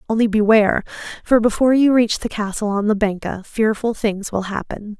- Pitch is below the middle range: No, high, 215 Hz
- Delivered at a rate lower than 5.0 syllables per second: No, 5.5 syllables/s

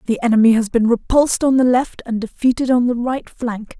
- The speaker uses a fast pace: Yes, fast, 220 wpm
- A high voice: Yes, high, 240 Hz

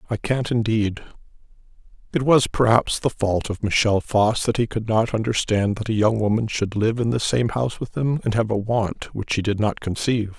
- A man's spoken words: Yes, male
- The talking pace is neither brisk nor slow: No, fast, 215 wpm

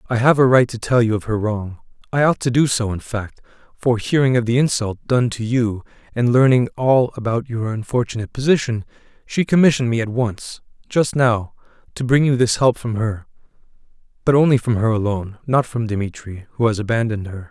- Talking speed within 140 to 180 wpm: No, average, 190 wpm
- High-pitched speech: No, low, 120 Hz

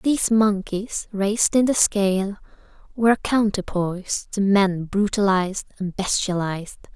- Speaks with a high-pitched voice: Yes, high, 200 Hz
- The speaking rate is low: Yes, slow, 120 wpm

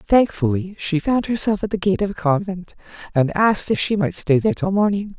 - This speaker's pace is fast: Yes, fast, 220 wpm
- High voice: Yes, high, 195 Hz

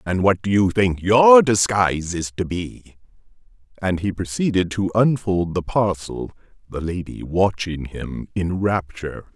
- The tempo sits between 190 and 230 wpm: No, average, 145 wpm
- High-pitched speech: No, very low, 95 Hz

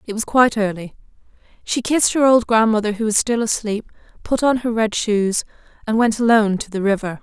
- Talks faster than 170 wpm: Yes, average, 200 wpm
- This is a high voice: Yes, high, 220 Hz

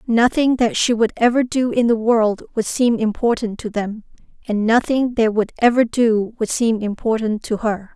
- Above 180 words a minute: Yes, average, 190 wpm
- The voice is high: Yes, high, 225 Hz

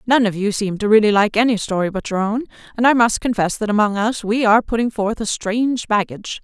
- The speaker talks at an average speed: No, fast, 245 wpm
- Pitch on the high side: Yes, high, 215 Hz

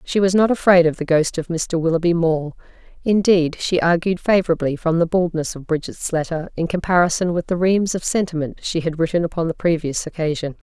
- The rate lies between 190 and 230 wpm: Yes, average, 195 wpm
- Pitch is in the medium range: Yes, medium, 170 Hz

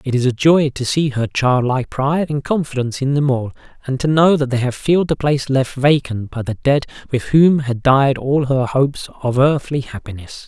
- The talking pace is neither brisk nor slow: No, fast, 220 wpm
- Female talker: No, male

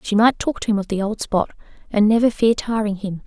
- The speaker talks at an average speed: No, fast, 255 wpm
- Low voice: No, high, 215 Hz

